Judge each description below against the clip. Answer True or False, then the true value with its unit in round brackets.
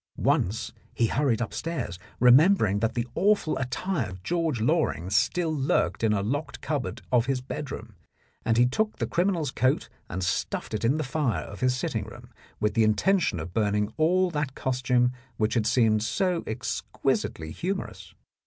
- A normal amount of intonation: False (6.4 semitones)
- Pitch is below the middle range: True (125 Hz)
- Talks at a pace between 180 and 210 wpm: False (165 wpm)